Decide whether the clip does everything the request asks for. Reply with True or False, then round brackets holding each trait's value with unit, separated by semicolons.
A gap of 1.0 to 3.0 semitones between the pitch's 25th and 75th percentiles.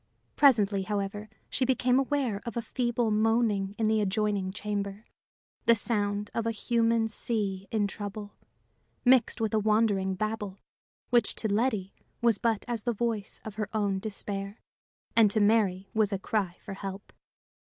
True (2.4 semitones)